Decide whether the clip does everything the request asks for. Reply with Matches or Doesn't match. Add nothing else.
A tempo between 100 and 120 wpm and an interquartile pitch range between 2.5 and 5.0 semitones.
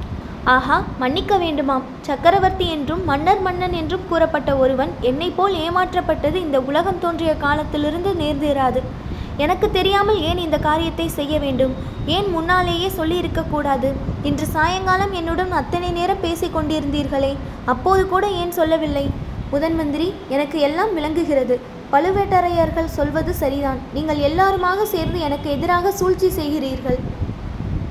Matches